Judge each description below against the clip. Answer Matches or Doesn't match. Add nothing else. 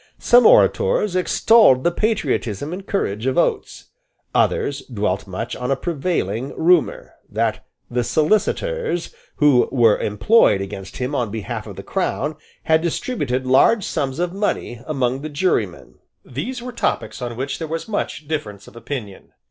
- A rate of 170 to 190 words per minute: Doesn't match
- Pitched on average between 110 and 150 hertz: Matches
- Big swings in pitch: Matches